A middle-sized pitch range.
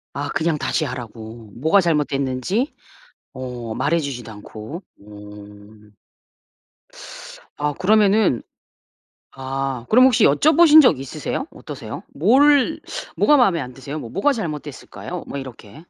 No: wide, 8.5 semitones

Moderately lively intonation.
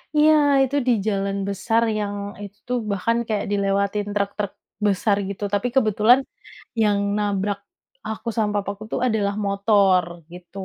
No: narrow, 1.5 semitones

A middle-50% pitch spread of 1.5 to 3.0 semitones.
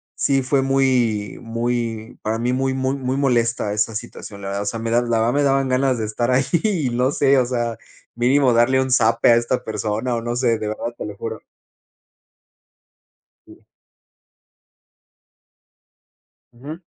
Yes: narrow, 2.6 semitones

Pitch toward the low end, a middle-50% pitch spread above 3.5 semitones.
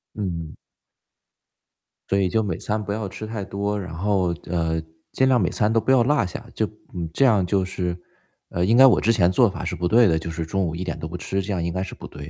Yes: very low, 95 Hz; average, 3.9 semitones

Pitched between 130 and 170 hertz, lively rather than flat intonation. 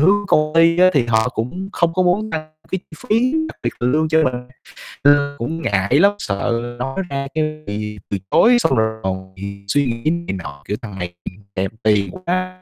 Yes: medium, 140 Hz; wide, 8.2 semitones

